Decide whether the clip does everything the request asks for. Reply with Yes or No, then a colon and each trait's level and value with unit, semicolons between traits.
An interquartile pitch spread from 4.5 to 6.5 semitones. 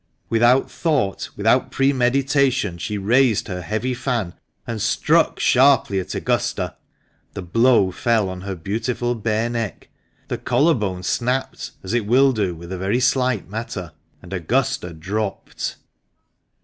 Yes: average, 4.8 semitones